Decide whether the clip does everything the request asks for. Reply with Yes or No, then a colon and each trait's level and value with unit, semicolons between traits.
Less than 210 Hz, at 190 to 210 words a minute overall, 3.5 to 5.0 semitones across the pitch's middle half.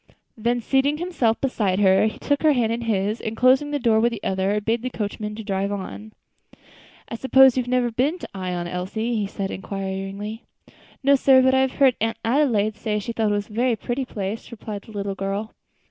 No: high, 220 Hz; fast, 205 wpm; average, 3.9 semitones